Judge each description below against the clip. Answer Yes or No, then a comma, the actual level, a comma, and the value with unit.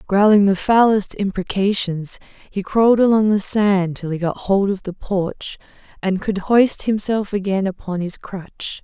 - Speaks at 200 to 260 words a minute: No, average, 165 wpm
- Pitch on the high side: Yes, high, 200 Hz